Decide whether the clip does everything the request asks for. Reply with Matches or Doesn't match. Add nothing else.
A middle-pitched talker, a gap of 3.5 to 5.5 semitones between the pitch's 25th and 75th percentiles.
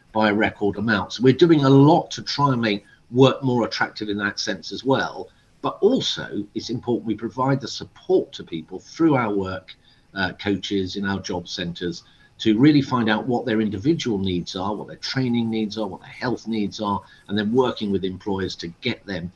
Doesn't match